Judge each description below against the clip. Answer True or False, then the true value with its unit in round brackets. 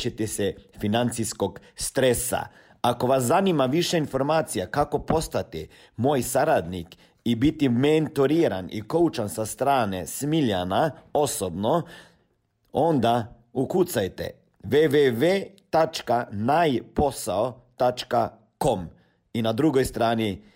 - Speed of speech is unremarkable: False (85 wpm)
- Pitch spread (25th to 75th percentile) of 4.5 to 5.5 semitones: True (4.8 semitones)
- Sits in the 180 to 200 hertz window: False (125 Hz)